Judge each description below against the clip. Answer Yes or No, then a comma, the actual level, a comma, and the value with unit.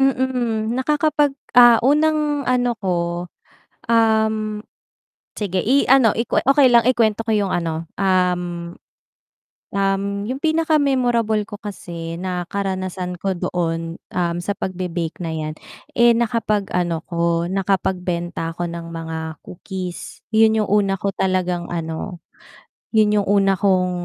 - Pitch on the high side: Yes, high, 195 Hz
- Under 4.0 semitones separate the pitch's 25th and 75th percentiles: No, average, 5.0 semitones